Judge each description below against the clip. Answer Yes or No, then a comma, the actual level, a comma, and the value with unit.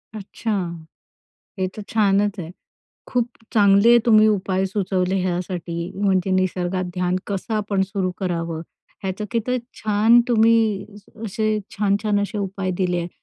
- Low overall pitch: No, high, 195 Hz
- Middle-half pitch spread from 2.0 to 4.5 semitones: Yes, narrow, 2.6 semitones